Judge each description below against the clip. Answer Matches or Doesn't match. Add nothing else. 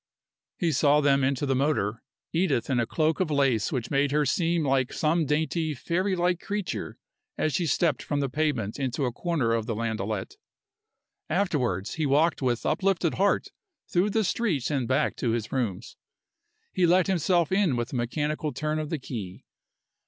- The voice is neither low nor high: Matches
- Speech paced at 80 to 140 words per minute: Doesn't match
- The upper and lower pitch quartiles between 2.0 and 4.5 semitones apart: Doesn't match